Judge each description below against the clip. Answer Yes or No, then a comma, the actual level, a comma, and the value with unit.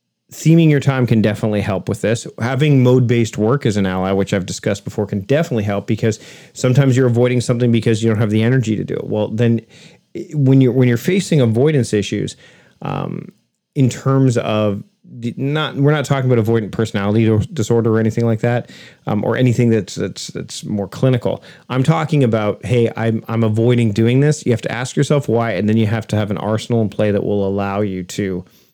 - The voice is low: Yes, low, 115 Hz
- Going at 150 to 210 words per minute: Yes, fast, 205 wpm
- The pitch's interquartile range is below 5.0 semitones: Yes, average, 3.4 semitones